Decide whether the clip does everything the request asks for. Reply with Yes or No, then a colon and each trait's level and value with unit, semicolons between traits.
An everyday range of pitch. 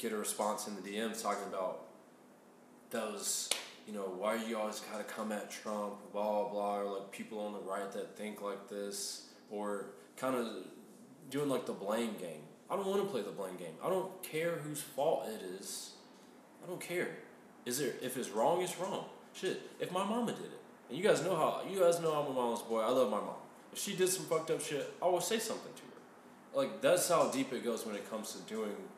No: wide, 8.5 semitones